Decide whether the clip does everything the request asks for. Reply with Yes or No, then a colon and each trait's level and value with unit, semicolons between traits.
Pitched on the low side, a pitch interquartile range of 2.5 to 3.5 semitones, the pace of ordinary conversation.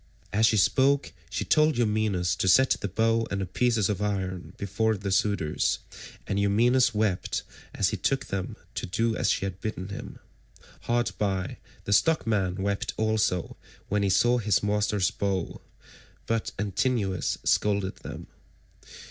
Yes: low, 105 Hz; average, 2.9 semitones; average, 150 wpm